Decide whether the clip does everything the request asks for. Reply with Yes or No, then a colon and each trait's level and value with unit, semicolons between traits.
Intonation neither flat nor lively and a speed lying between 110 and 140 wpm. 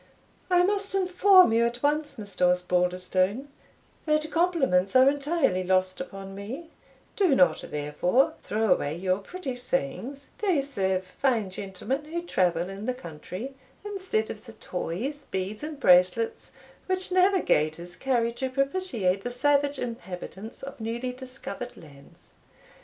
No: wide, 7.6 semitones; slow, 135 wpm